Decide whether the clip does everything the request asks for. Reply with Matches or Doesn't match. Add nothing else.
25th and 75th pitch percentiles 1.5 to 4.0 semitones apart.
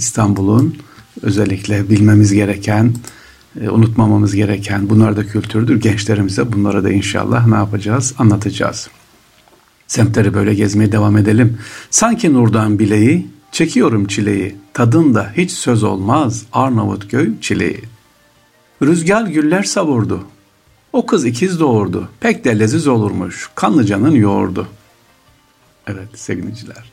Matches